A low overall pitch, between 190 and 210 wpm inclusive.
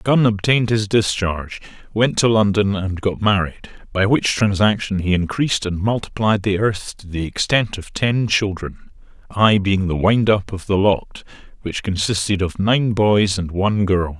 No: low, 100 Hz; average, 175 wpm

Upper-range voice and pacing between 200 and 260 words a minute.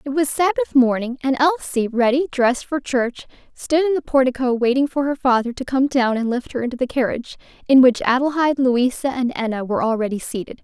Yes: very high, 260 Hz; fast, 205 wpm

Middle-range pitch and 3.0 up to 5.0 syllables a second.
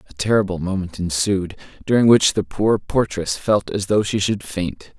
No: very low, 95 Hz; 4.7 syllables/s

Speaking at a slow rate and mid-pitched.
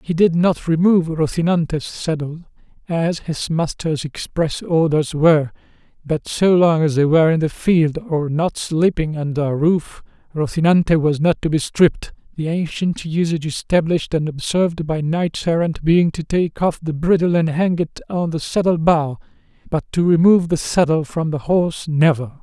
No: average, 165 wpm; medium, 160 Hz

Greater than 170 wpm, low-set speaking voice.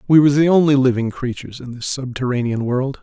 Yes: average, 200 wpm; low, 130 Hz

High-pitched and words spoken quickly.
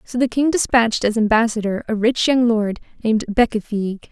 No: high, 225 Hz; average, 175 wpm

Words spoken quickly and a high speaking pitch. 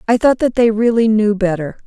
Yes: fast, 225 wpm; high, 220 Hz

